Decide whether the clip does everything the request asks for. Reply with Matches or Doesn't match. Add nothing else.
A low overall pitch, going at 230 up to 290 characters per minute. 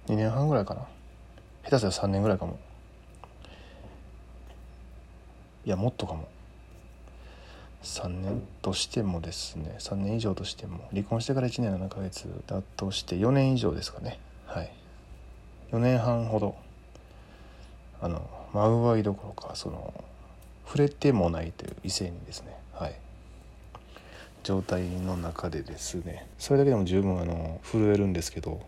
Matches